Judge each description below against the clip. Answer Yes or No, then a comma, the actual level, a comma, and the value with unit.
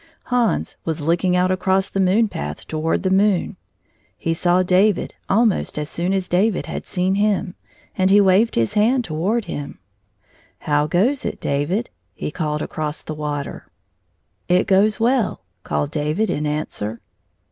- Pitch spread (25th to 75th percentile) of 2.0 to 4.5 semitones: No, average, 5.1 semitones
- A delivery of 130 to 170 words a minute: Yes, average, 160 wpm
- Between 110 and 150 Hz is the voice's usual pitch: No, medium, 180 Hz